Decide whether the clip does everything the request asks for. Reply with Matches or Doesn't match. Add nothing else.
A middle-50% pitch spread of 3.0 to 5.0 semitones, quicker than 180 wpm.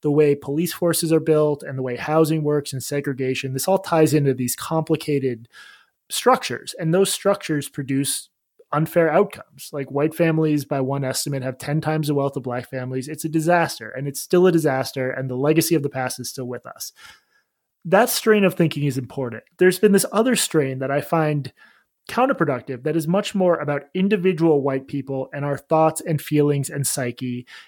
Matches